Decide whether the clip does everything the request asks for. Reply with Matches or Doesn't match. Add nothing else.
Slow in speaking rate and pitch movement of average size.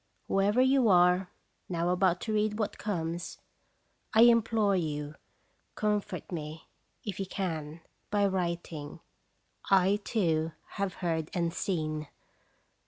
Matches